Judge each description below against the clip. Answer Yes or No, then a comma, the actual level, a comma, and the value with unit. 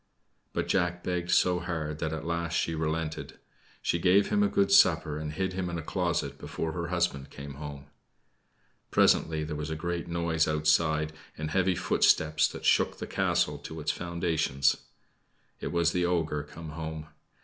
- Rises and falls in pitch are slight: Yes, narrow, 2.2 semitones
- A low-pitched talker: Yes, very low, 80 Hz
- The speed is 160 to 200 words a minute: Yes, average, 170 wpm